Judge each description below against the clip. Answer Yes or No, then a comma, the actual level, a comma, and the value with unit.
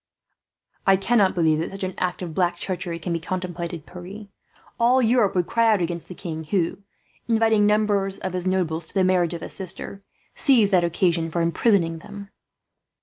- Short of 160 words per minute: No, average, 185 wpm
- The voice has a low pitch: No, medium, 185 Hz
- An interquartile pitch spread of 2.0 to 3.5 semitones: Yes, average, 3.0 semitones